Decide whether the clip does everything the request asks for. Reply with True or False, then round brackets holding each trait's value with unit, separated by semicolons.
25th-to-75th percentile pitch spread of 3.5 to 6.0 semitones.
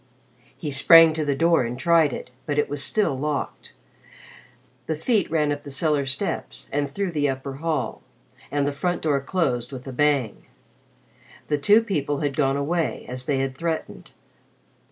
False (3.1 semitones)